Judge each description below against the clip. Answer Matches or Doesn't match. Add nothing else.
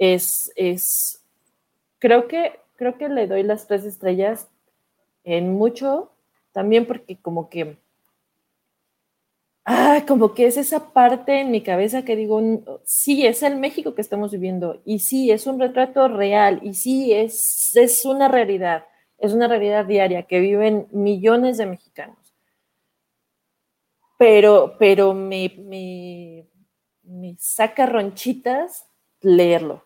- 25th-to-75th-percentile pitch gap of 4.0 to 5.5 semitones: Matches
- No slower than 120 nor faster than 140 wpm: Matches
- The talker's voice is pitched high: Matches